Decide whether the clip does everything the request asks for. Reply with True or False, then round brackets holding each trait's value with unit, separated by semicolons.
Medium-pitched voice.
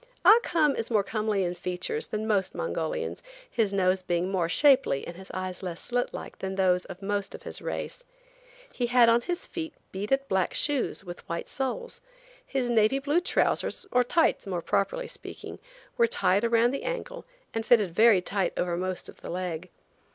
False (215 Hz)